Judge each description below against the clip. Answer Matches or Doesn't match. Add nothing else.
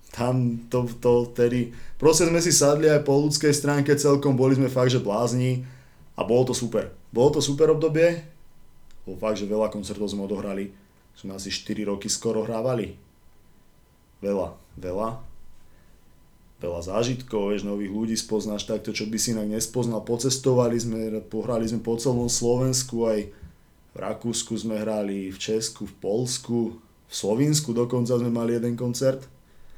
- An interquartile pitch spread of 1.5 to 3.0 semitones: Doesn't match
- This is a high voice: Doesn't match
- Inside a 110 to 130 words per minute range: Doesn't match